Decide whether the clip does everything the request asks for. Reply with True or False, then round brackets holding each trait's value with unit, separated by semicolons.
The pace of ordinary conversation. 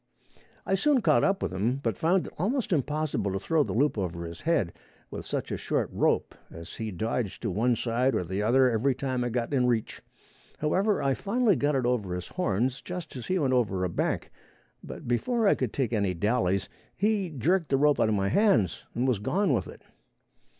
False (215 wpm)